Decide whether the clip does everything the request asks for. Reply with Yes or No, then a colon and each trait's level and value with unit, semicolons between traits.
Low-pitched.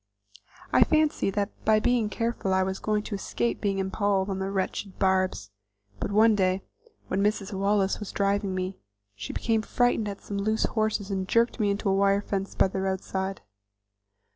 No: high, 200 Hz